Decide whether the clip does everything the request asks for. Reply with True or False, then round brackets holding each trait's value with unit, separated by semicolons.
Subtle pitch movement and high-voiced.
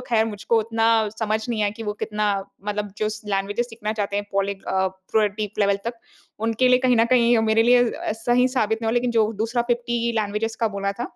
True (2.3 semitones; 220 Hz)